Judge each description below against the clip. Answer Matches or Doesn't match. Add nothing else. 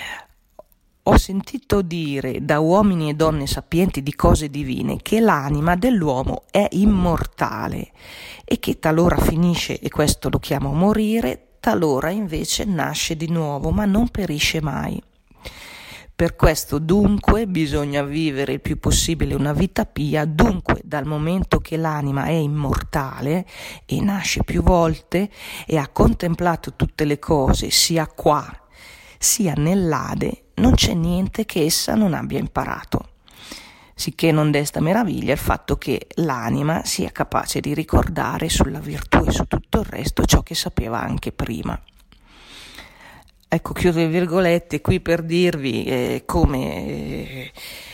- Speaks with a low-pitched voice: Doesn't match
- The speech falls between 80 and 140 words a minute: Matches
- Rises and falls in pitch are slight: Doesn't match